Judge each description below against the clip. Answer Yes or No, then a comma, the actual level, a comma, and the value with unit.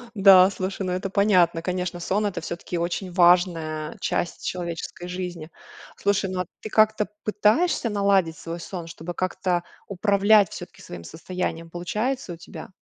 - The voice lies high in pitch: No, medium, 180 Hz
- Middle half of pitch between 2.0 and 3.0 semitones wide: Yes, narrow, 2.6 semitones